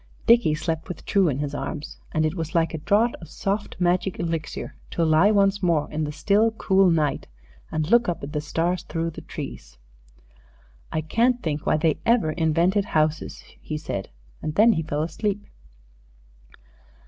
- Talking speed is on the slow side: No, average, 170 wpm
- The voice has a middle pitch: Yes, medium, 165 Hz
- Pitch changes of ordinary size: Yes, average, 4.3 semitones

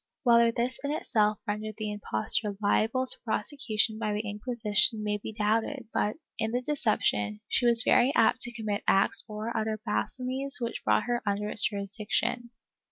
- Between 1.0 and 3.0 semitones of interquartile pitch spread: Yes, narrow, 2.5 semitones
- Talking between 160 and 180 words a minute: Yes, average, 175 wpm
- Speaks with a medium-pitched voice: No, high, 220 Hz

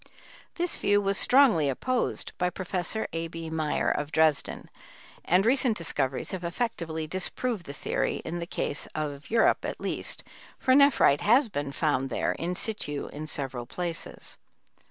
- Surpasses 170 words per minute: No, average, 155 wpm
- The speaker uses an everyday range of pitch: No, wide, 6.3 semitones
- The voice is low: No, medium, 170 Hz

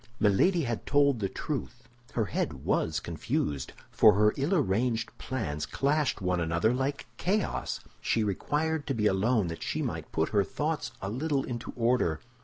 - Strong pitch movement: Yes, wide, 6.4 semitones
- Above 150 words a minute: Yes, average, 160 wpm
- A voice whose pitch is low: Yes, low, 120 Hz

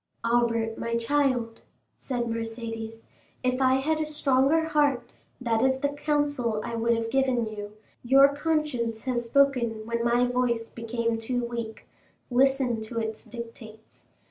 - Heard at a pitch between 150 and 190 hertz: No, high, 240 Hz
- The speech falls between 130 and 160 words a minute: Yes, average, 145 wpm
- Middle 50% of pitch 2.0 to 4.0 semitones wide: Yes, average, 2.8 semitones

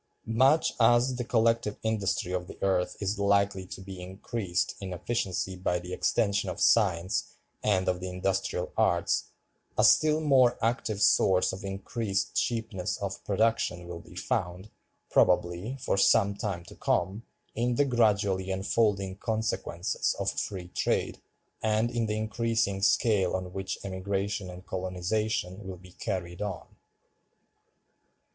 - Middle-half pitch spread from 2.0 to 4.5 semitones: Yes, average, 3.3 semitones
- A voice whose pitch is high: No, low, 100 Hz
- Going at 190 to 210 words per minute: No, average, 140 wpm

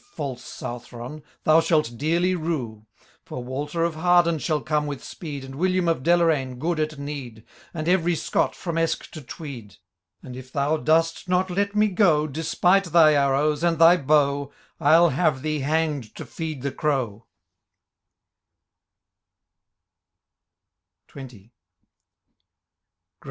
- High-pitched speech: No, medium, 155 Hz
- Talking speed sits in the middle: No, slow, 130 wpm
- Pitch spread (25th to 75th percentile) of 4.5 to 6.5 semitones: No, average, 3.5 semitones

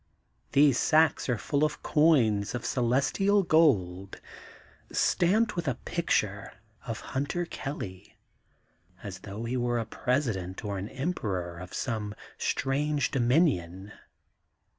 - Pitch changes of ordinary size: No, wide, 6.9 semitones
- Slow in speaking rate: Yes, slow, 120 wpm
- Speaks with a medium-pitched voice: No, low, 125 Hz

